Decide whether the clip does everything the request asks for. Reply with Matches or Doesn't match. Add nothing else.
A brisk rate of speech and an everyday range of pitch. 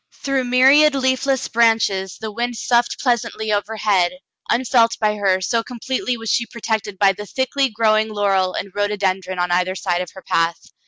Doesn't match